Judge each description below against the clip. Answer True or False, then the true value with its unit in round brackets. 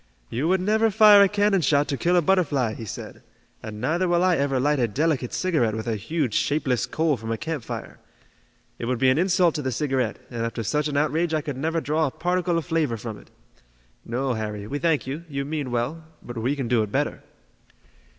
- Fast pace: True (220 wpm)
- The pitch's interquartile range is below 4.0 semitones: False (5.6 semitones)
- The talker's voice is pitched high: False (145 Hz)